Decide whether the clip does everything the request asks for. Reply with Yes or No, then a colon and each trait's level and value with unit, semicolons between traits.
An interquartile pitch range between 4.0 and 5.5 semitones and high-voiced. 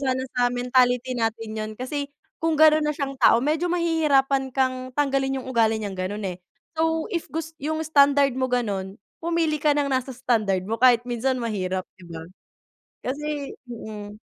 Yes: average, 4.3 semitones; very high, 260 Hz